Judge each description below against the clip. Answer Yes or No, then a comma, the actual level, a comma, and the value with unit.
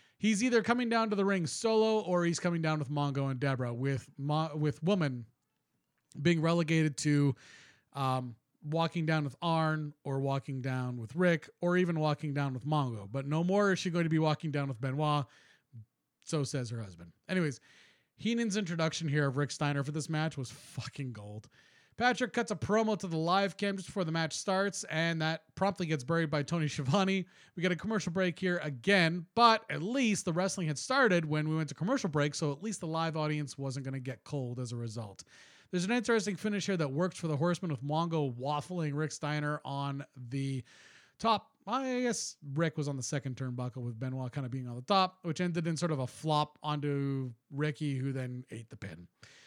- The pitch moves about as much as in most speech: Yes, average, 4.7 semitones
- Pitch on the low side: No, medium, 155 Hz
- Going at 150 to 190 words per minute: No, fast, 205 wpm